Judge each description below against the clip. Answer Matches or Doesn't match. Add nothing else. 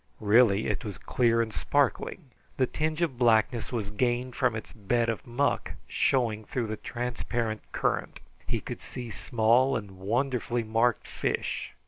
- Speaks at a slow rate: Doesn't match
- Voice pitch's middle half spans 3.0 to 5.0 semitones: Doesn't match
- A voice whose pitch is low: Matches